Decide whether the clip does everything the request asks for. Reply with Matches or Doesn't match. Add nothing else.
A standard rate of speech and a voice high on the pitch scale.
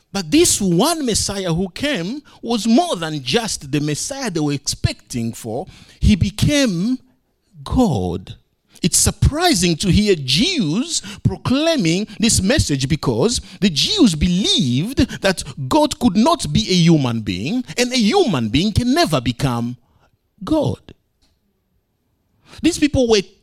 Doesn't match